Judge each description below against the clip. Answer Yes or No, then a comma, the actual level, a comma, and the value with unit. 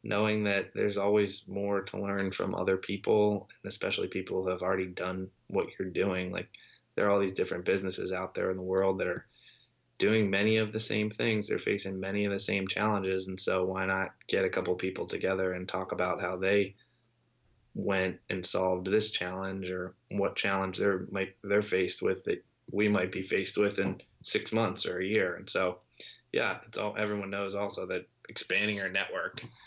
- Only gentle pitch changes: Yes, narrow, 1.8 semitones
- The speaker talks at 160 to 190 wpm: No, average, 200 wpm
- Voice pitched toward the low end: Yes, very low, 95 Hz